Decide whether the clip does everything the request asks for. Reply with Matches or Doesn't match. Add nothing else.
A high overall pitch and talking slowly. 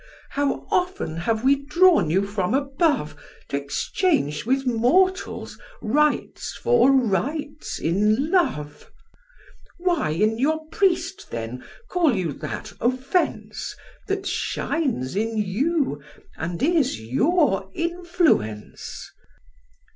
Matches